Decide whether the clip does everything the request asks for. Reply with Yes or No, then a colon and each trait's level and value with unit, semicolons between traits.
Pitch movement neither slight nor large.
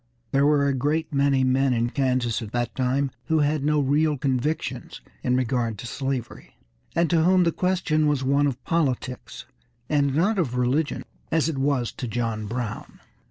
Yes: average, 3.3 semitones